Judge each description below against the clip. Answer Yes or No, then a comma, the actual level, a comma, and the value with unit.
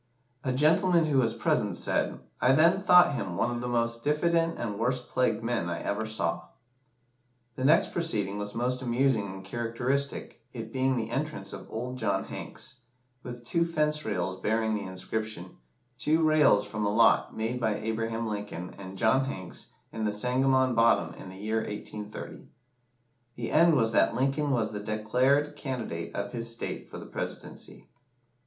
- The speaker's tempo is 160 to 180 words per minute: Yes, average, 170 wpm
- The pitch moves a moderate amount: Yes, average, 4.0 semitones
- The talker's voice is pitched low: Yes, low, 115 Hz